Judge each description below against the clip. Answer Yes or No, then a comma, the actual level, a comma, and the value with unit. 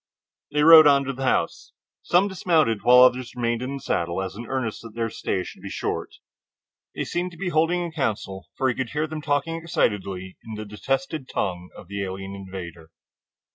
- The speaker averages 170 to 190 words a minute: No, average, 200 wpm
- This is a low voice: Yes, low, 125 Hz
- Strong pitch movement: Yes, wide, 7.5 semitones